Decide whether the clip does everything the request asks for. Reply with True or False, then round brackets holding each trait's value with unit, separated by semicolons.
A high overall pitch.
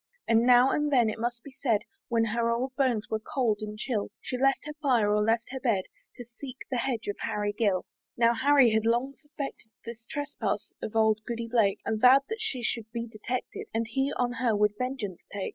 True (235 Hz)